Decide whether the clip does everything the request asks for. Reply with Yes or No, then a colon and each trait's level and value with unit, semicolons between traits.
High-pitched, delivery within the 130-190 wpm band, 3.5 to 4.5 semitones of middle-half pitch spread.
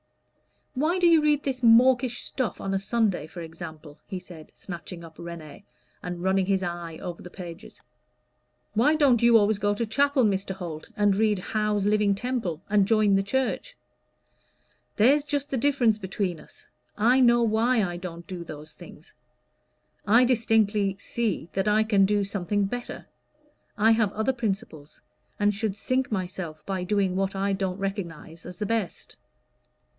Yes: high, 205 Hz; average, 165 wpm; average, 4.2 semitones